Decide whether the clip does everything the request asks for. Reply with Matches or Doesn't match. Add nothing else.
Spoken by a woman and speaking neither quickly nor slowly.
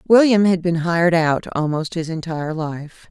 Matches